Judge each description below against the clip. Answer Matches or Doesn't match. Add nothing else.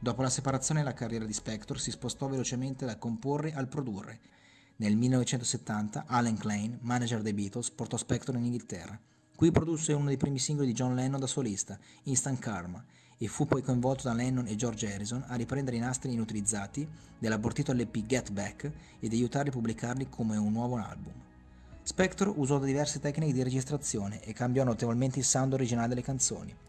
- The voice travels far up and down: Doesn't match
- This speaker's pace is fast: Matches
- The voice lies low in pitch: Matches